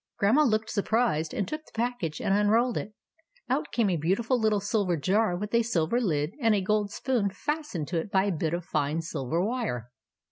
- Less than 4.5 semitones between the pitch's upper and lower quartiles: No, average, 5.2 semitones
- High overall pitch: Yes, high, 205 Hz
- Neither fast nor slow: No, fast, 220 wpm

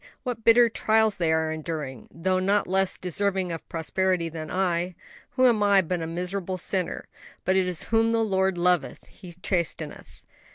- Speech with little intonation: No, average, 3.0 semitones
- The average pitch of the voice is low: No, medium, 185 Hz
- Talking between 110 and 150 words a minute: No, average, 165 wpm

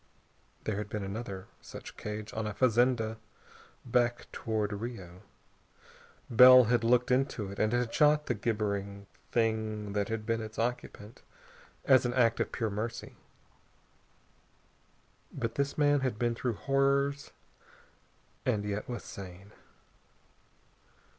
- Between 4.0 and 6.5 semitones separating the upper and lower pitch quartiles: No, average, 2.9 semitones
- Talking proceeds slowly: Yes, slow, 125 wpm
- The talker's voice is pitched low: Yes, low, 115 Hz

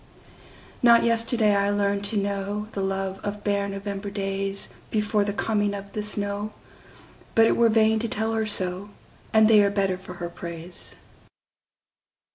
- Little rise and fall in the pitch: Yes, narrow, 1.5 semitones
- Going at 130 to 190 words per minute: Yes, average, 140 wpm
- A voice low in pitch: No, high, 205 Hz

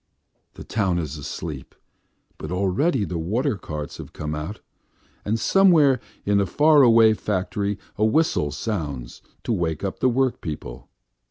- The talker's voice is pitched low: Yes, low, 100 Hz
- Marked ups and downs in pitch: Yes, wide, 6.9 semitones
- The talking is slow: No, average, 145 wpm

